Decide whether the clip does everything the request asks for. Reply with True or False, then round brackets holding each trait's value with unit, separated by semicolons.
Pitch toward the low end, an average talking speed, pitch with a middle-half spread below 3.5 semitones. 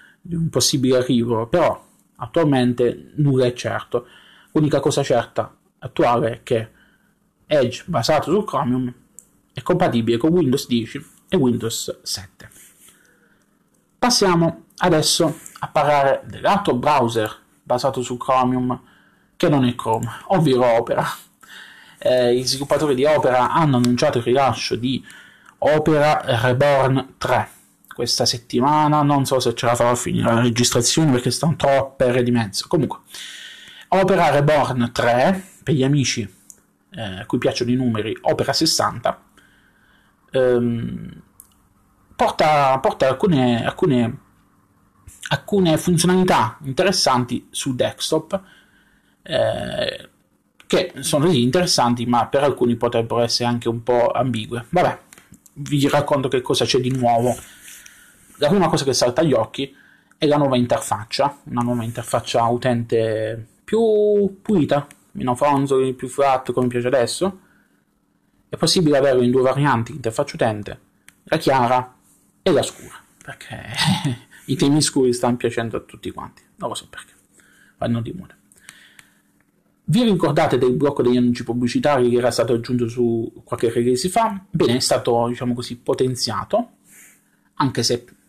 False (125 Hz; 135 wpm; 3.8 semitones)